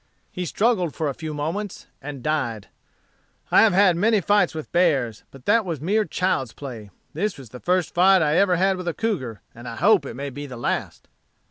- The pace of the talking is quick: Yes, fast, 210 wpm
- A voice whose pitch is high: No, medium, 165 Hz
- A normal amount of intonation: No, wide, 5.9 semitones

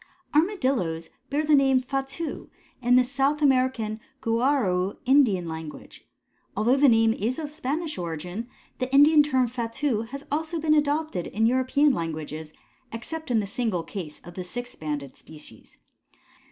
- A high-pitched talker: Yes, very high, 250 Hz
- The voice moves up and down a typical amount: No, wide, 7.3 semitones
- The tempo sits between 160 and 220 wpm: No, average, 150 wpm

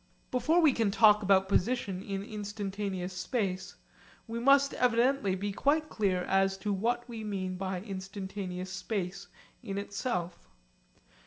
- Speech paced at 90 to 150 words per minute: Yes, slow, 135 wpm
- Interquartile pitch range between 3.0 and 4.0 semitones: Yes, average, 3.4 semitones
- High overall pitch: Yes, high, 200 Hz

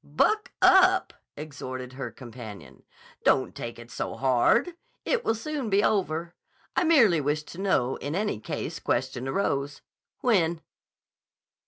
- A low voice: No, medium, 155 Hz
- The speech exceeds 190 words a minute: No, slow, 135 wpm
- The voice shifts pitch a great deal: Yes, wide, 8.5 semitones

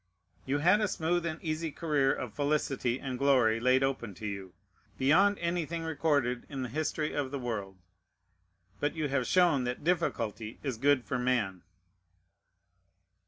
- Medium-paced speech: Yes, average, 155 wpm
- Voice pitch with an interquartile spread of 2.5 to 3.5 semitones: No, average, 4.4 semitones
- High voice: No, medium, 140 Hz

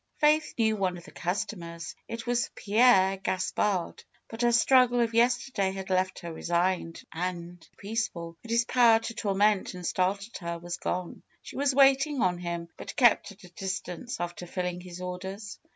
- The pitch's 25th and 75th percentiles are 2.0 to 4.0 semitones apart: No, average, 4.6 semitones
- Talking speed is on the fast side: No, average, 180 wpm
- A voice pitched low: No, high, 190 Hz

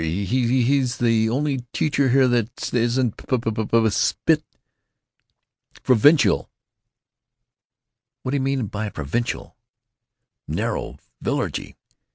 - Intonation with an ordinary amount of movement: Yes, average, 3.0 semitones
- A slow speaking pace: Yes, slow, 100 wpm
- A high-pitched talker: No, low, 120 Hz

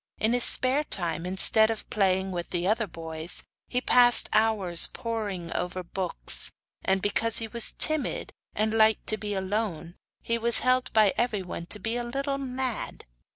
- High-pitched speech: Yes, high, 215 Hz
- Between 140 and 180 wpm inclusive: Yes, average, 165 wpm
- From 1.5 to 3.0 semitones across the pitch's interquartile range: No, average, 4.2 semitones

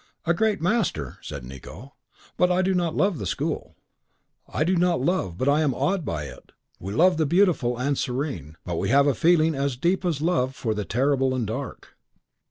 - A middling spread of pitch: No, wide, 6.4 semitones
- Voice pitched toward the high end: No, medium, 145 Hz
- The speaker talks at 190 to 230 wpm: Yes, average, 200 wpm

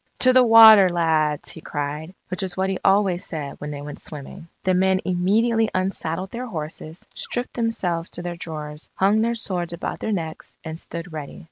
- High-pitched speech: No, medium, 175 Hz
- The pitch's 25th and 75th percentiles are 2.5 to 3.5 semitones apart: No, average, 3.9 semitones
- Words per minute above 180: Yes, average, 190 wpm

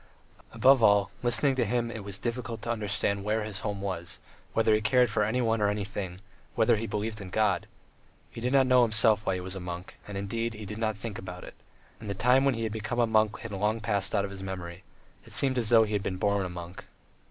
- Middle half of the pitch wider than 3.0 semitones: No, narrow, 2.6 semitones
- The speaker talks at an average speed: No, fast, 245 wpm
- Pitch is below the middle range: Yes, low, 105 Hz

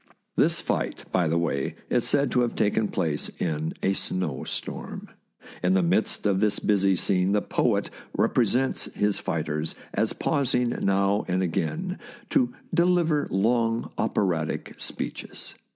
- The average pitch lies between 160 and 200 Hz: No, low, 100 Hz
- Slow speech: No, average, 145 wpm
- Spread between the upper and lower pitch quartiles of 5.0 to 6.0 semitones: Yes, wide, 5.4 semitones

